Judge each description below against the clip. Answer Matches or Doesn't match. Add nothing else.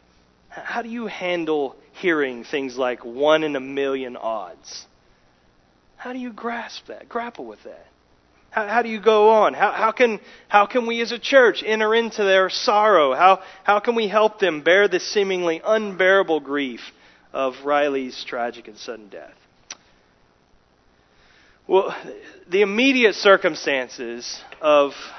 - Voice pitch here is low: Doesn't match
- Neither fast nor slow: Matches